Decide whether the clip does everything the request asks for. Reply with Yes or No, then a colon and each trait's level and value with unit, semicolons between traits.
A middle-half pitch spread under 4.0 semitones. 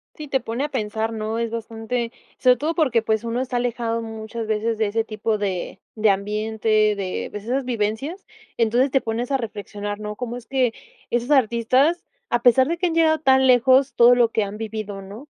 Yes: average, 2.9 semitones